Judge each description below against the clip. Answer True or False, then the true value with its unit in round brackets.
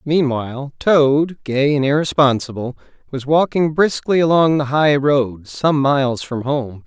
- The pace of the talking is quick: False (140 wpm)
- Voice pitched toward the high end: False (140 Hz)